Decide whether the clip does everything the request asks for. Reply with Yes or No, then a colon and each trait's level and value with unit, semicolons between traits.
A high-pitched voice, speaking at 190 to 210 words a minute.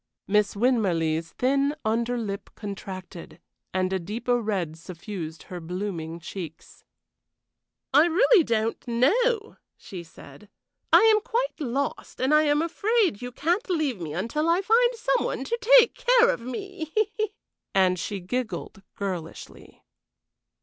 No: high, 235 Hz; slow, 135 wpm